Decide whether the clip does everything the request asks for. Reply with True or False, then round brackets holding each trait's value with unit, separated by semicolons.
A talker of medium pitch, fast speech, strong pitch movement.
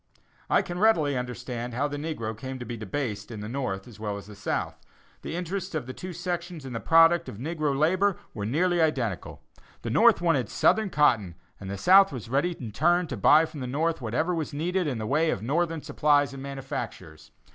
True (145 Hz; 220 wpm; 6.2 semitones)